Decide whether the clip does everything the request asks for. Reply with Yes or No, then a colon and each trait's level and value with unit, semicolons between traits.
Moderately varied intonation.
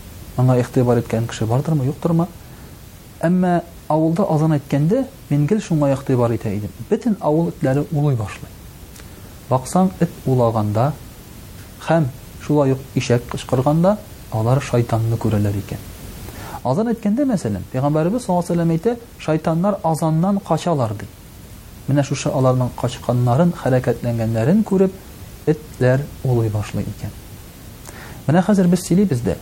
No: wide, 6.3 semitones